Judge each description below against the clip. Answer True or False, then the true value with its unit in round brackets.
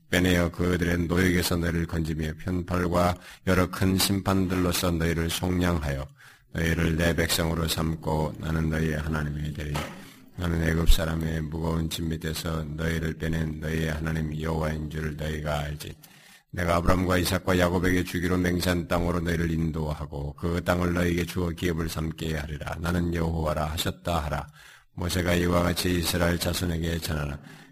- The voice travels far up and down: False (1.8 semitones)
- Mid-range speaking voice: False (85 Hz)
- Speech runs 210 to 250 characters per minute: False (355 characters per minute)